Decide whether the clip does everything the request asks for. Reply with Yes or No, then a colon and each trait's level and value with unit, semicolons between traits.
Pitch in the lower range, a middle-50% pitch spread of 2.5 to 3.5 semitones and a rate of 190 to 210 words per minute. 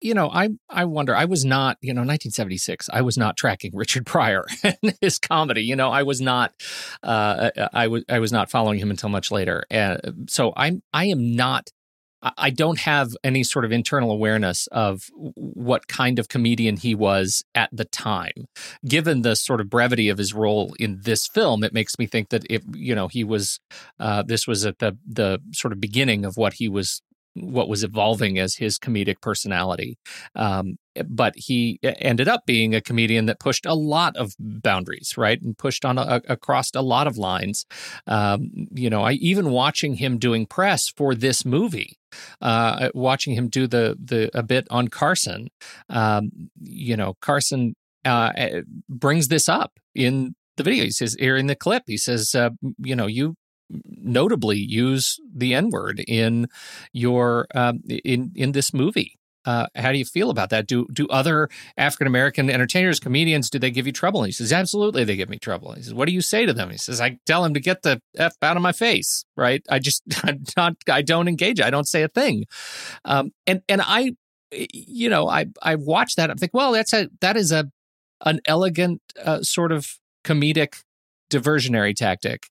No: low, 125 Hz; wide, 5.4 semitones; average, 200 wpm